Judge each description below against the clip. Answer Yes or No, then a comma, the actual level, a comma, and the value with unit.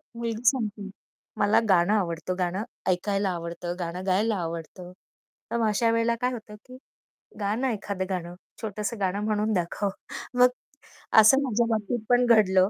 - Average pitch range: Yes, average, 3.8 semitones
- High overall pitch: Yes, high, 205 Hz